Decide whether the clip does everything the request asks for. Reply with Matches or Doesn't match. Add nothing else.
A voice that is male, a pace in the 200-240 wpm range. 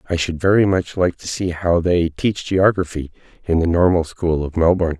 Matches